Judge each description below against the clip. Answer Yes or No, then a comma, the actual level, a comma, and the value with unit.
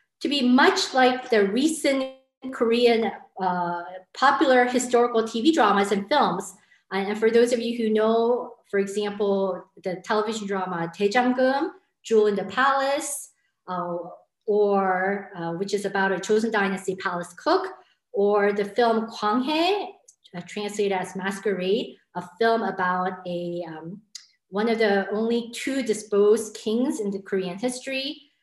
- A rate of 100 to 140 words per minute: Yes, slow, 135 wpm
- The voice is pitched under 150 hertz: No, high, 215 Hz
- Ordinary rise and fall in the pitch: Yes, average, 4.6 semitones